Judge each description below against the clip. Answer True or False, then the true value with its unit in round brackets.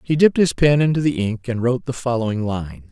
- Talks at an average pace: False (245 wpm)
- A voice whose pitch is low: True (125 Hz)